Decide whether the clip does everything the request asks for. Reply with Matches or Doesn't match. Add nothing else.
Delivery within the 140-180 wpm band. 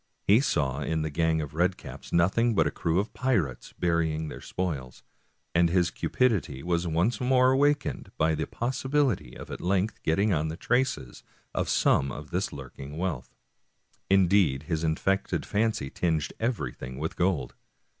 Matches